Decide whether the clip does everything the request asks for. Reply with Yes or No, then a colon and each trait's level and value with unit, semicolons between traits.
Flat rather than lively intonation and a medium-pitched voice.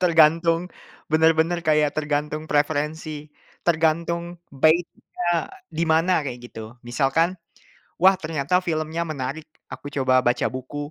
Yes: narrow, 2.2 semitones; medium, 155 Hz